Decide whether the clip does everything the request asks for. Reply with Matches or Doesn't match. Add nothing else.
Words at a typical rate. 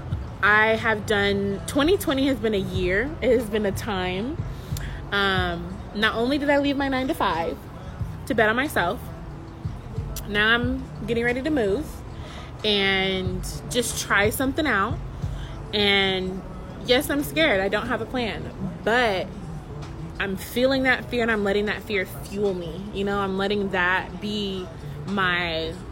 Matches